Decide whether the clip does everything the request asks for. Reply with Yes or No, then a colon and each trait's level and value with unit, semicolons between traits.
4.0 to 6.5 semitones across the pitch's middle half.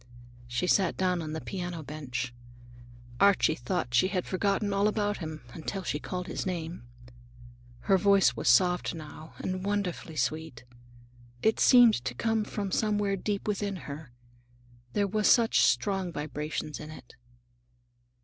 Yes: average, 4.6 semitones